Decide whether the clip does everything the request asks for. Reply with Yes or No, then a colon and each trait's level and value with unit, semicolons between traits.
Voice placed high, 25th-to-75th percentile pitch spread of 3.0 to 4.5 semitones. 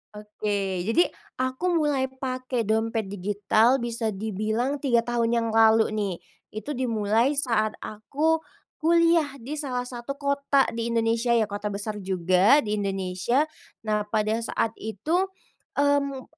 Yes: high, 230 Hz; average, 4.2 semitones